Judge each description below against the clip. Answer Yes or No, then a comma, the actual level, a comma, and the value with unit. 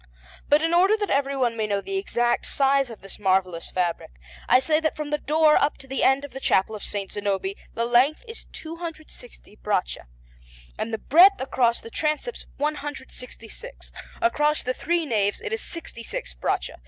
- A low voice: No, very high, 270 Hz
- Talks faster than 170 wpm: Yes, average, 180 wpm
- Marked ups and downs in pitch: Yes, wide, 6.2 semitones